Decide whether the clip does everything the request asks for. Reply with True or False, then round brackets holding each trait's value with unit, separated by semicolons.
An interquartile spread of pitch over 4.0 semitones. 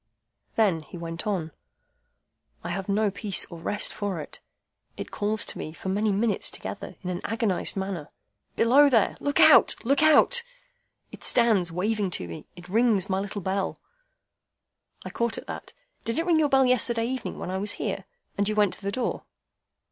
False (3.7 semitones)